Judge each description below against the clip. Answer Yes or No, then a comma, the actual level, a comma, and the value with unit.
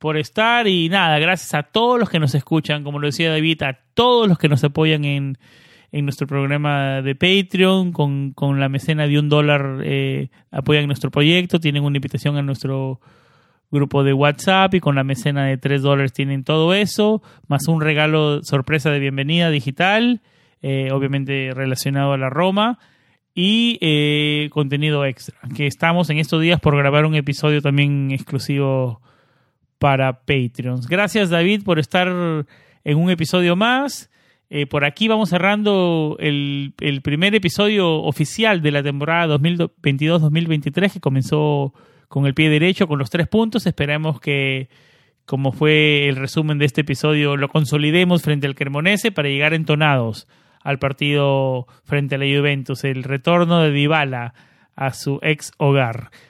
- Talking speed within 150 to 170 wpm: Yes, average, 160 wpm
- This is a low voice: No, medium, 150 Hz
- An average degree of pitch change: Yes, average, 3.1 semitones